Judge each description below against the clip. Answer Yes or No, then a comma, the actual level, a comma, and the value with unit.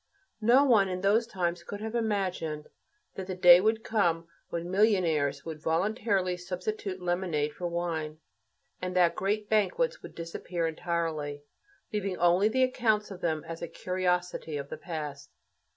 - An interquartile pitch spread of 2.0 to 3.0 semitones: No, average, 3.8 semitones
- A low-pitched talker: No, medium, 180 Hz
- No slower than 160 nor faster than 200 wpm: No, average, 150 wpm